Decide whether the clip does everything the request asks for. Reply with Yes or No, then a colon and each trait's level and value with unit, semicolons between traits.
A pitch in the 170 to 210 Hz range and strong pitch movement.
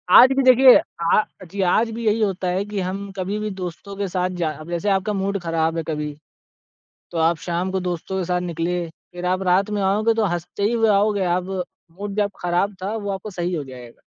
No: high, 190 Hz; average, 2.9 semitones